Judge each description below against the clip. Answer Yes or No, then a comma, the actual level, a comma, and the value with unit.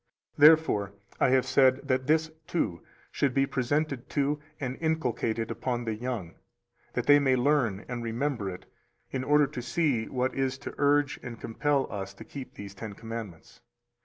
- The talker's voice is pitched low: Yes, low, 130 Hz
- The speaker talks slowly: No, average, 165 wpm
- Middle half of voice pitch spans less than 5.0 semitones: Yes, average, 4.1 semitones